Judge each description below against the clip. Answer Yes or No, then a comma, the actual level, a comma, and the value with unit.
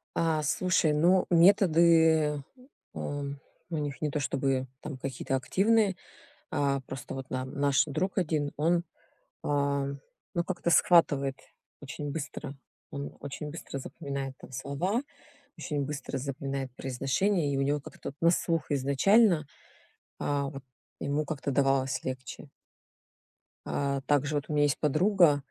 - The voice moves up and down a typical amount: Yes, average, 3.1 semitones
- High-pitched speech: No, medium, 145 Hz